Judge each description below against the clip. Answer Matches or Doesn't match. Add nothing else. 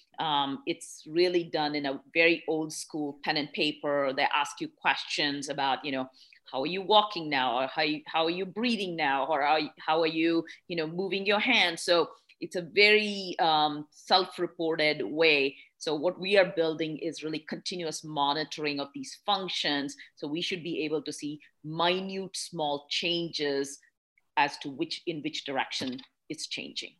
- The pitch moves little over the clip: Doesn't match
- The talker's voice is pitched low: Doesn't match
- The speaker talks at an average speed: Matches